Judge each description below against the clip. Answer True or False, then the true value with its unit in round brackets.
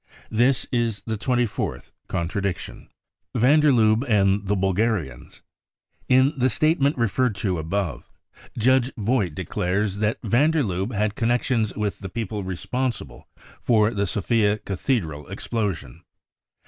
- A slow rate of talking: True (130 wpm)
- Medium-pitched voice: False (110 Hz)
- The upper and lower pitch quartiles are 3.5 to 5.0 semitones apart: True (4.0 semitones)